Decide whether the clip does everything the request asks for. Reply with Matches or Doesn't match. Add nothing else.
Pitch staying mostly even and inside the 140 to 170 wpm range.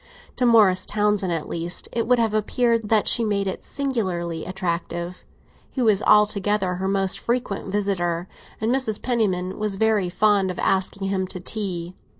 Doesn't match